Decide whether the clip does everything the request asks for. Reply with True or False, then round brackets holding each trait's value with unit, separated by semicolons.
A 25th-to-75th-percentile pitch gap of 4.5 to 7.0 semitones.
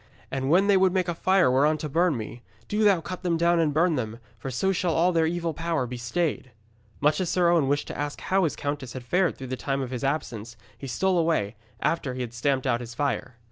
True (5.1 semitones)